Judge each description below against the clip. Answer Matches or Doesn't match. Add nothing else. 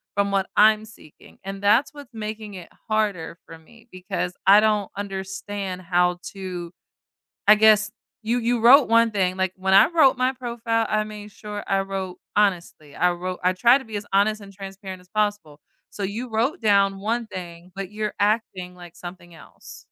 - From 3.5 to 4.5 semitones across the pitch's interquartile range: Doesn't match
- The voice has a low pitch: Doesn't match